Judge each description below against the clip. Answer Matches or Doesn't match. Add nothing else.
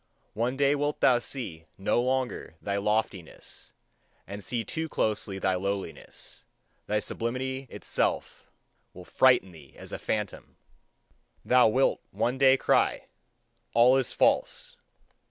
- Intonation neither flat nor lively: Matches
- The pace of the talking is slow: Matches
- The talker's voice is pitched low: Matches